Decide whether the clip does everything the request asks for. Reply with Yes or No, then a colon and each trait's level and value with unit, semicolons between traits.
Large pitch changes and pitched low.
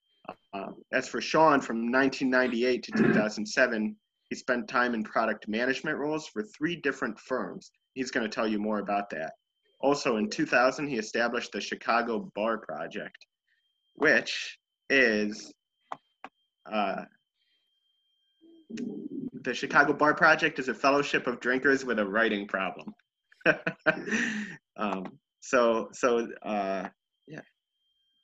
Yes: wide, 5.9 semitones; low, 125 Hz